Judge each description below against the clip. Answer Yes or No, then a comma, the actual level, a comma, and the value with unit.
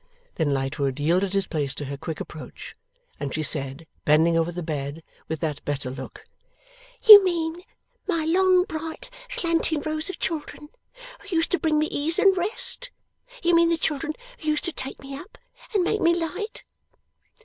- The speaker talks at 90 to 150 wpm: No, average, 175 wpm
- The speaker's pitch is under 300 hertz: No, very high, 305 Hz